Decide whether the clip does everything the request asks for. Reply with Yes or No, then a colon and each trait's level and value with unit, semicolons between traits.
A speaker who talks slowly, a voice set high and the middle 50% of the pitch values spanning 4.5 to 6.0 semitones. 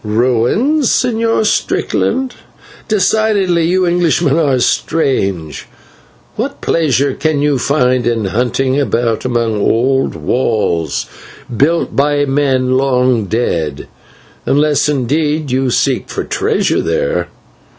No: slow, 105 wpm; low, 135 Hz; average, 5.2 semitones